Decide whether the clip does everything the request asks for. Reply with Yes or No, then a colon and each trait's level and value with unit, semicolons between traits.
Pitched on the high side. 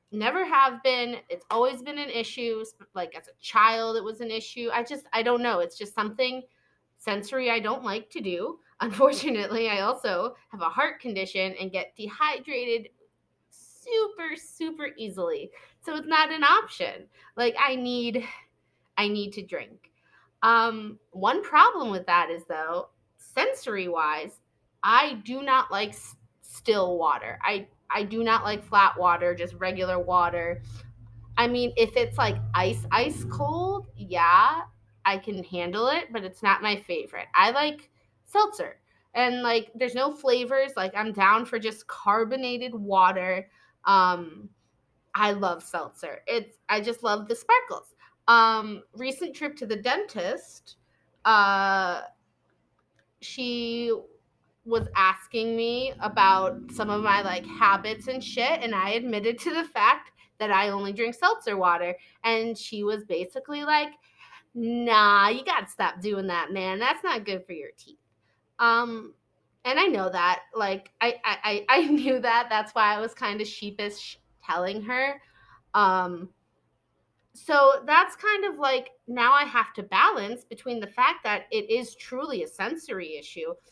Yes: high, 225 Hz